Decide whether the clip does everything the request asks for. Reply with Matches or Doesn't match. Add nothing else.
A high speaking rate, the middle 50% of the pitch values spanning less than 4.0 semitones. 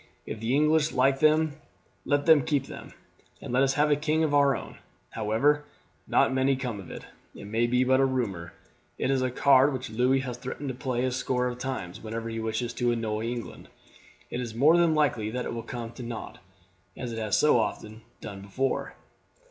Matches